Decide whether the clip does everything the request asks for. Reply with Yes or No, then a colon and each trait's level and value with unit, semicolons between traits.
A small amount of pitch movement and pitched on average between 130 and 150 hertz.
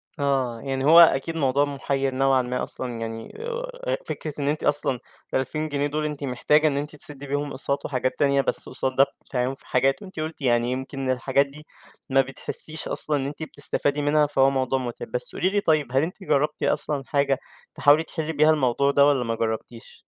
Yes: narrow, 2.2 semitones; medium, 140 Hz